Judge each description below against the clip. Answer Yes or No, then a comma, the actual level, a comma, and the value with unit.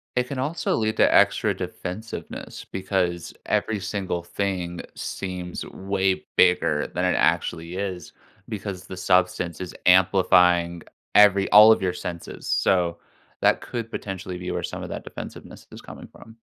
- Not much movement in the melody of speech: Yes, narrow, 2.2 semitones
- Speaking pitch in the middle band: No, very low, 95 Hz